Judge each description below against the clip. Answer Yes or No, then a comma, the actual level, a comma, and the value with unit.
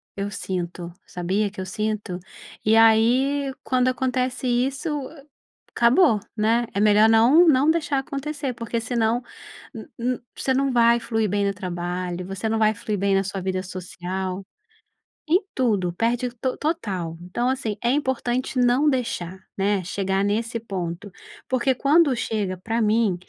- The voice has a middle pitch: No, high, 225 Hz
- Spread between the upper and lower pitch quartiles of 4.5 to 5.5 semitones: Yes, average, 4.8 semitones